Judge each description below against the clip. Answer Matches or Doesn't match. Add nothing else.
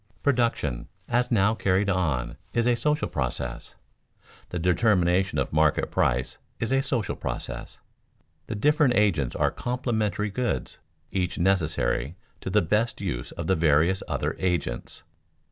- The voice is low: Matches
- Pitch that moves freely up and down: Matches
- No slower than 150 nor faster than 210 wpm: Doesn't match